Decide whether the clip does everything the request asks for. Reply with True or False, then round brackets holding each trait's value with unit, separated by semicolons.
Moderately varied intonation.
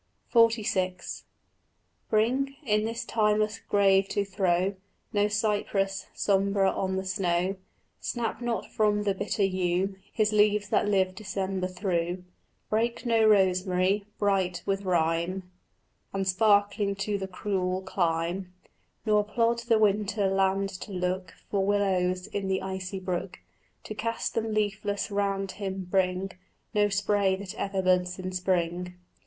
False (2.0 semitones)